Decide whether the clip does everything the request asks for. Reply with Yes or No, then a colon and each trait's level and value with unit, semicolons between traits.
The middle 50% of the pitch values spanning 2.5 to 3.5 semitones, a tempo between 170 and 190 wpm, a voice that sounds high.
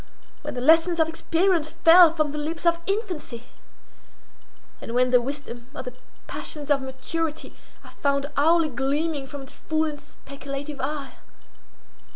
No: average, 3.1 semitones; average, 150 wpm; very high, 295 Hz